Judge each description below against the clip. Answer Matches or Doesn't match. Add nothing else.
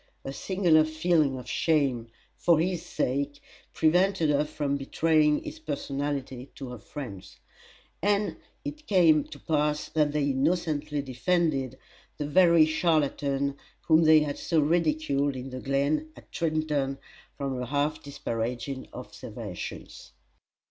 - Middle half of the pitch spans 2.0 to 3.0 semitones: Matches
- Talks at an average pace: Doesn't match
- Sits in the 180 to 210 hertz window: Doesn't match